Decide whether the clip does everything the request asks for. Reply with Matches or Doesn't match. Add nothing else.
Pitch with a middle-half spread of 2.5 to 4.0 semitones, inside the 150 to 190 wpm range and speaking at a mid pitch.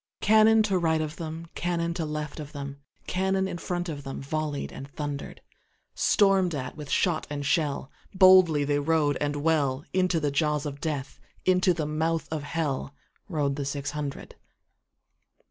Doesn't match